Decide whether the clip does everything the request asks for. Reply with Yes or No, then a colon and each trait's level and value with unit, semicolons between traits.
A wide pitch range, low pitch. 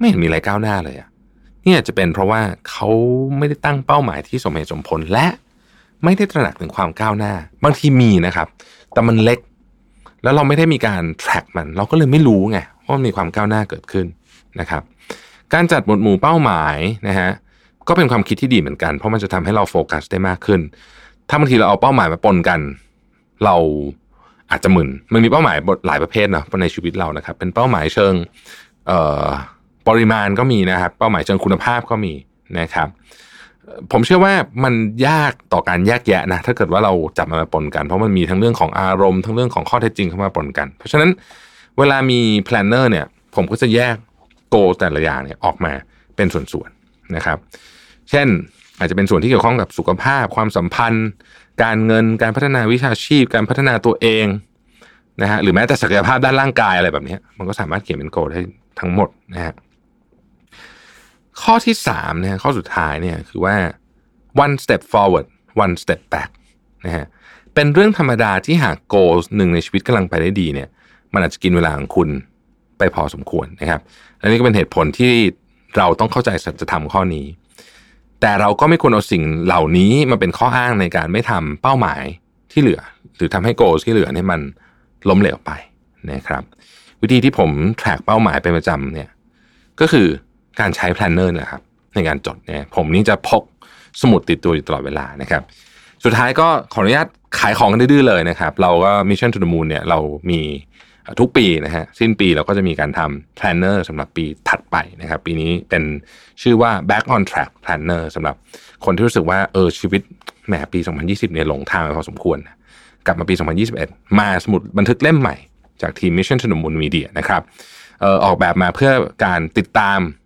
Yes: wide, 5.9 semitones; low, 100 Hz